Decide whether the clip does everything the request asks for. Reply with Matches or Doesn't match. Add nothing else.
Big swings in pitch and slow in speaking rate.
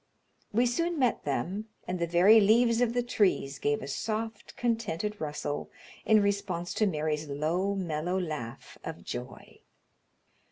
Doesn't match